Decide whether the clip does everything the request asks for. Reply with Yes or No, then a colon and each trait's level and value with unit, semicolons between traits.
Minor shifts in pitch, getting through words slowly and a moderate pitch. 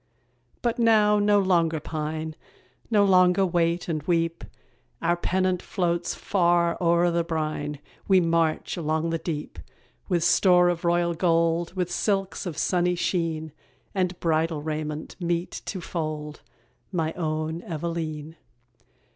Yes: narrow, 2.0 semitones; slow, 130 wpm; medium, 170 Hz